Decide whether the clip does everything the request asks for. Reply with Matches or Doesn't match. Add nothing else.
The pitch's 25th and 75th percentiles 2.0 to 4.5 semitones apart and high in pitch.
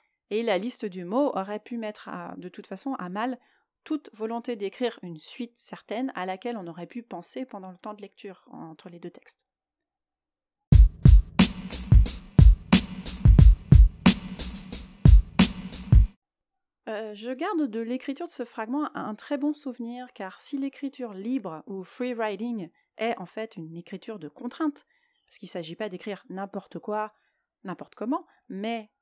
Doesn't match